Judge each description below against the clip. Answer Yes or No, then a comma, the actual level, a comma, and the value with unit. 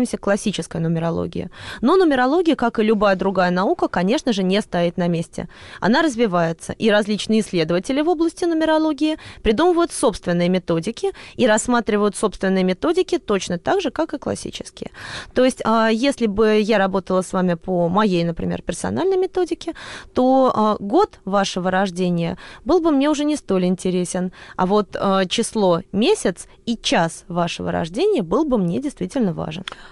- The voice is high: Yes, high, 215 Hz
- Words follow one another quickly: No, average, 145 wpm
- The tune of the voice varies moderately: No, wide, 7.3 semitones